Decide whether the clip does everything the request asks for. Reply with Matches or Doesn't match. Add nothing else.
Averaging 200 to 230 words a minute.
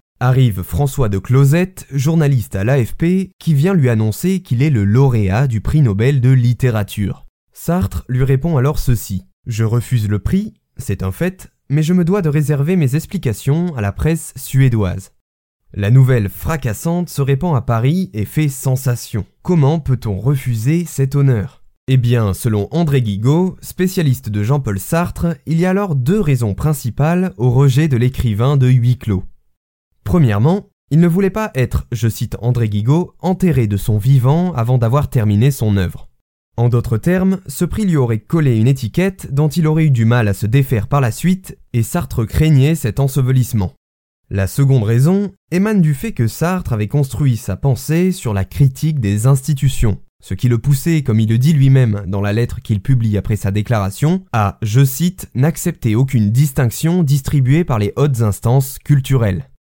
Doesn't match